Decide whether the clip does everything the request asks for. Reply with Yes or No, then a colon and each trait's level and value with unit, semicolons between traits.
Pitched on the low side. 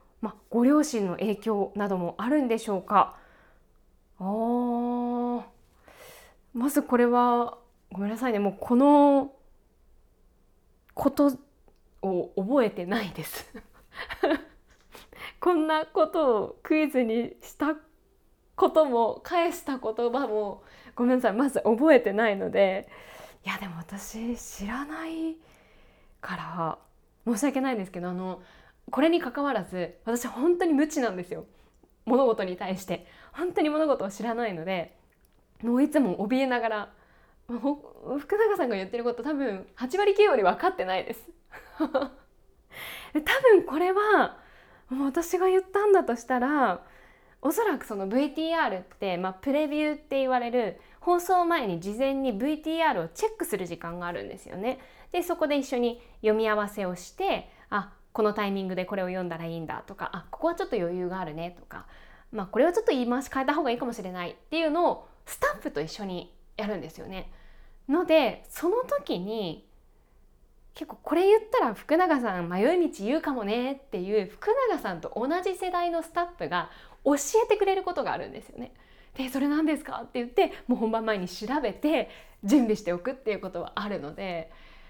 No: very high, 255 Hz